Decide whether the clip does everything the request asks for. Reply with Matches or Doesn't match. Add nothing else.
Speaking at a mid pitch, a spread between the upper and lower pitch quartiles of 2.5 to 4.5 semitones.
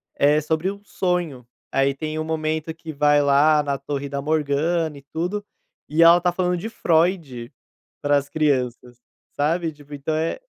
Matches